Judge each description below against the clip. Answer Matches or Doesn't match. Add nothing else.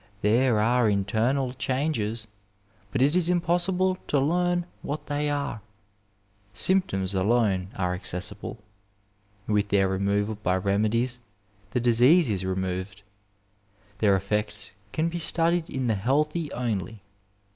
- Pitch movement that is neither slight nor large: Doesn't match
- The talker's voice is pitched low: Matches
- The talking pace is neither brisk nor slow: Doesn't match